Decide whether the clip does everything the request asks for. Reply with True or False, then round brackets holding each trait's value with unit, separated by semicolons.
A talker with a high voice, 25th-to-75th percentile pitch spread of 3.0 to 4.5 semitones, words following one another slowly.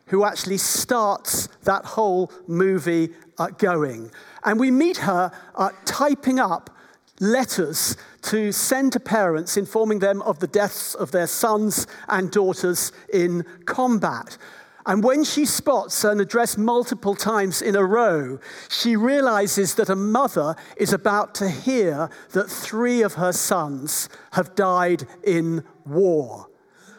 True (200 Hz; 3.7 semitones; 130 wpm)